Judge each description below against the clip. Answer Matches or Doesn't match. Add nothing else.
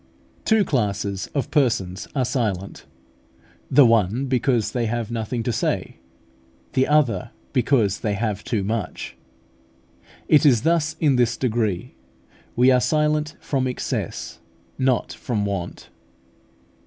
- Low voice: Matches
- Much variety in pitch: Doesn't match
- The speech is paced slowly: Matches